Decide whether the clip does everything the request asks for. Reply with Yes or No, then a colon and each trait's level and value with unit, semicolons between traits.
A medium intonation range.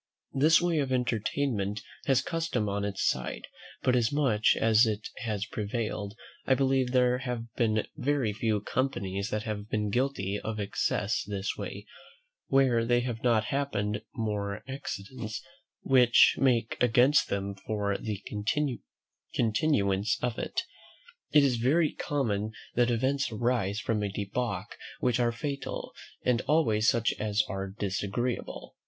Yes: average, 3.7 semitones